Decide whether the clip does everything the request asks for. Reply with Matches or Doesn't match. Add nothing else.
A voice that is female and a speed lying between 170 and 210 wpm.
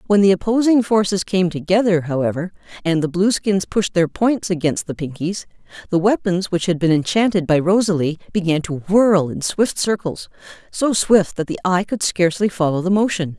Matches